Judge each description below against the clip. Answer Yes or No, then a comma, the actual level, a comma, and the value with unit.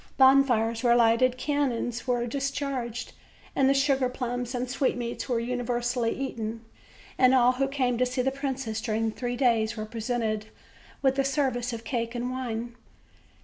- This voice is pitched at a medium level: No, high, 245 Hz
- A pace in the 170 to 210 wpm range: No, average, 150 wpm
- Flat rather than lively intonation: Yes, narrow, 2.3 semitones